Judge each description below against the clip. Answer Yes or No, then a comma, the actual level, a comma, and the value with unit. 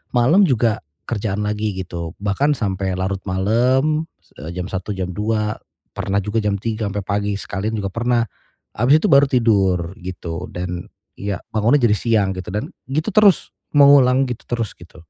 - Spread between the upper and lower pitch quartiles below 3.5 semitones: No, average, 4.3 semitones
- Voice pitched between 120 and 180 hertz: No, low, 105 Hz